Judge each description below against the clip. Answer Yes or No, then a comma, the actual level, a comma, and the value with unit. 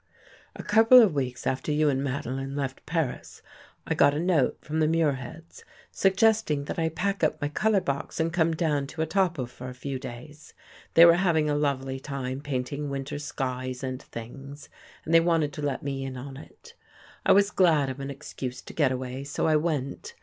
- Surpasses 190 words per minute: Yes, average, 200 wpm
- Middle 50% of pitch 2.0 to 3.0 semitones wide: No, average, 3.5 semitones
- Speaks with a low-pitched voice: No, medium, 145 Hz